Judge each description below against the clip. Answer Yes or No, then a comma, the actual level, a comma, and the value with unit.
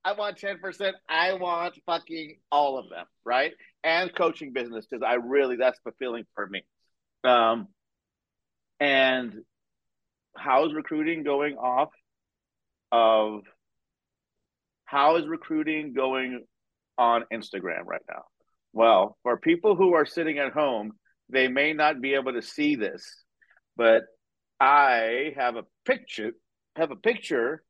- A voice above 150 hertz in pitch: No, medium, 140 Hz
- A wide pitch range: Yes, wide, 6.1 semitones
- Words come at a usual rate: No, slow, 130 wpm